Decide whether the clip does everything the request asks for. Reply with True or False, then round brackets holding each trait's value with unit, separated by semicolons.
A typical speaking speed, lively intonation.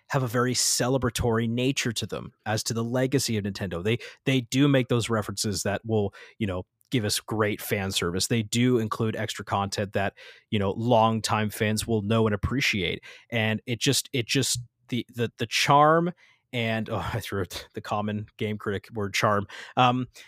False (185 wpm; 2.7 semitones)